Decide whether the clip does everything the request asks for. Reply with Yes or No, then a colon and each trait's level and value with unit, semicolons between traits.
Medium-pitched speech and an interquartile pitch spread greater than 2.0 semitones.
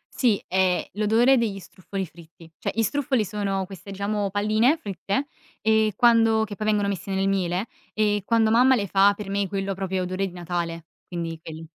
No: high, 200 Hz; average, 2.7 semitones